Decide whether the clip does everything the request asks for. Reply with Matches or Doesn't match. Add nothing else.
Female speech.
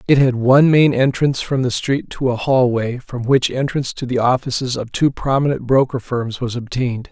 Doesn't match